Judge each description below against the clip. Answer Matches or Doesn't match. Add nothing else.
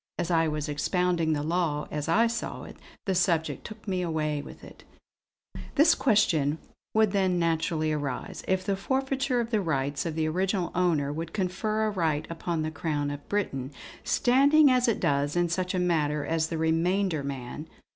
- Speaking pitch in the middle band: Matches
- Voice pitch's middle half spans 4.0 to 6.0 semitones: Matches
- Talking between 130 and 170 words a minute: Doesn't match